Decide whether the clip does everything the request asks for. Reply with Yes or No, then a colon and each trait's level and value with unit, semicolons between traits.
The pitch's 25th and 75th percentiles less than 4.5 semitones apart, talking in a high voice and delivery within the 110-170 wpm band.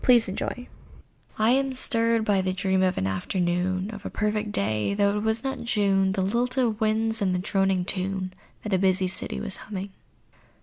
No: average, 2.9 semitones; high, 200 Hz; average, 185 wpm